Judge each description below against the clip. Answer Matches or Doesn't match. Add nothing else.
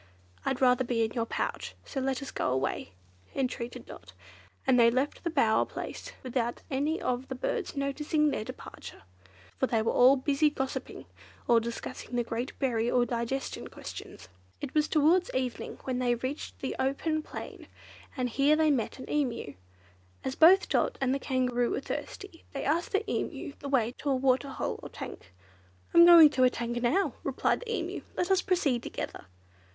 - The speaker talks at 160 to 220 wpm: Matches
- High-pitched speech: Matches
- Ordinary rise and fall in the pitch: Matches